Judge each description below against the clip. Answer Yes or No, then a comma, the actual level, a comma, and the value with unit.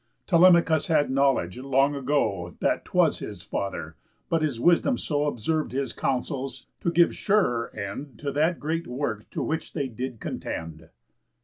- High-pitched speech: No, medium, 140 Hz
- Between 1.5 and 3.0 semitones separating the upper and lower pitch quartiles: No, average, 4.6 semitones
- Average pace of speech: Yes, average, 150 wpm